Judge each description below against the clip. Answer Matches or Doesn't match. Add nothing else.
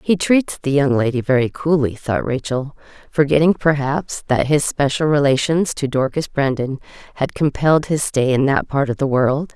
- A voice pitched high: Doesn't match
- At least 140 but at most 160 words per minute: Doesn't match